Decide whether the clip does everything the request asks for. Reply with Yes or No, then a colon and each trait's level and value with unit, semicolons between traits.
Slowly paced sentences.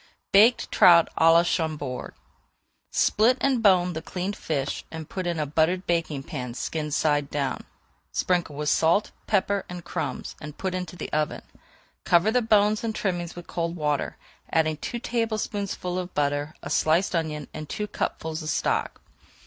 No: average, 165 wpm